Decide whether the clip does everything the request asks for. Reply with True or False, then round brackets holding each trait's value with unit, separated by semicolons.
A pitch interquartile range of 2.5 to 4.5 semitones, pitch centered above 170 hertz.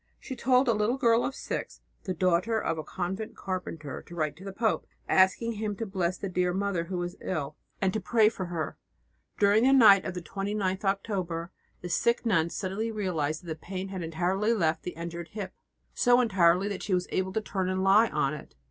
True (3.6 semitones; 190 Hz)